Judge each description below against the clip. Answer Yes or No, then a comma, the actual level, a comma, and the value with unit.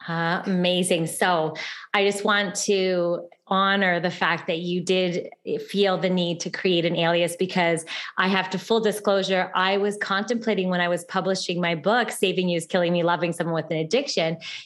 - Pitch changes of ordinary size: No, narrow, 2.2 semitones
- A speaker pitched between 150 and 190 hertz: Yes, medium, 185 Hz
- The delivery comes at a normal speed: Yes, average, 185 wpm